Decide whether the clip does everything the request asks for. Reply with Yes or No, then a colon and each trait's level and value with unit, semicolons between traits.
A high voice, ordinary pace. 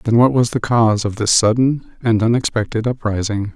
No: low, 115 Hz; average, 185 wpm